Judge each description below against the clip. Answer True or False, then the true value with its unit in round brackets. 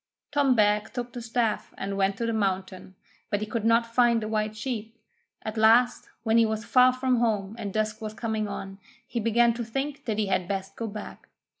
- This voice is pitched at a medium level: False (220 Hz)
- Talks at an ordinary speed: False (210 wpm)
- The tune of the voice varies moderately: False (2.1 semitones)